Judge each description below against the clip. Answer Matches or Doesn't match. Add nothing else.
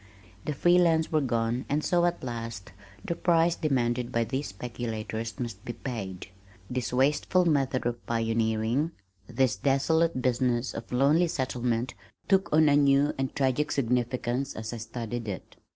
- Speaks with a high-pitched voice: Doesn't match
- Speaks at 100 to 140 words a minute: Doesn't match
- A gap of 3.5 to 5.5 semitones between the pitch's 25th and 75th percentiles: Matches